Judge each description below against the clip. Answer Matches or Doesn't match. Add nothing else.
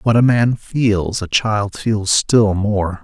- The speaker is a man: Matches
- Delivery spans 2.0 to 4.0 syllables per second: Matches